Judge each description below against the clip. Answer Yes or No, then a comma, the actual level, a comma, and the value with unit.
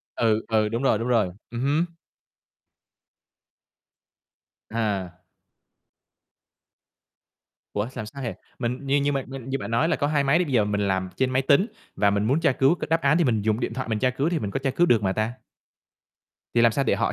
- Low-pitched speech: Yes, low, 125 Hz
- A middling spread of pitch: Yes, average, 4.3 semitones